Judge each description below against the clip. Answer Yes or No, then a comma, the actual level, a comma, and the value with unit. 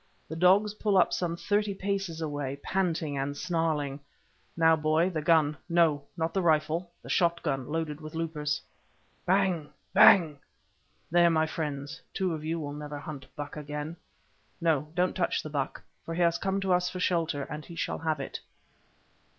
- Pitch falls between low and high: Yes, medium, 160 Hz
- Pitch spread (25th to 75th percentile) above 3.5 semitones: No, average, 2.9 semitones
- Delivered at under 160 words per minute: No, average, 170 wpm